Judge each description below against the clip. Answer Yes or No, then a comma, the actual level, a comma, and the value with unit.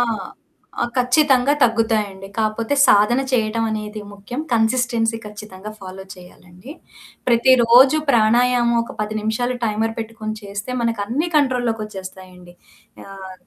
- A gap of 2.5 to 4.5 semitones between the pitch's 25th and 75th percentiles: Yes, average, 3.0 semitones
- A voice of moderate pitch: No, high, 225 Hz